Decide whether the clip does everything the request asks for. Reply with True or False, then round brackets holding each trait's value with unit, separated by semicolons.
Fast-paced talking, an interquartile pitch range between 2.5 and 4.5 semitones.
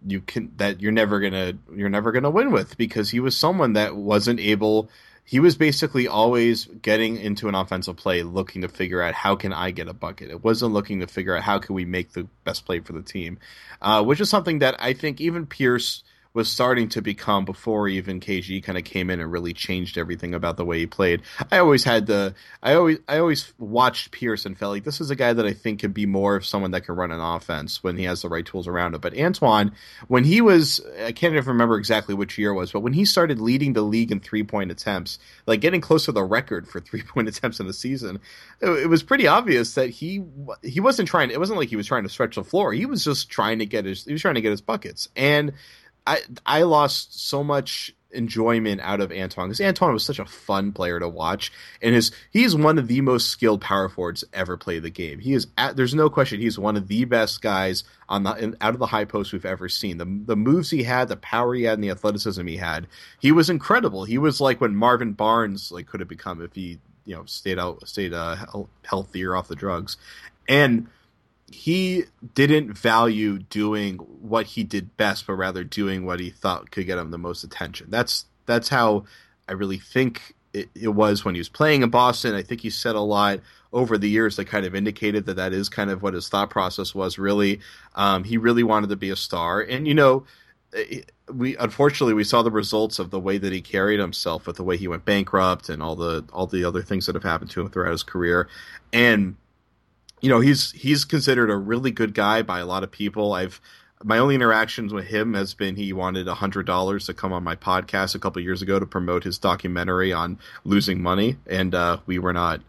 True (235 wpm; 4.2 semitones)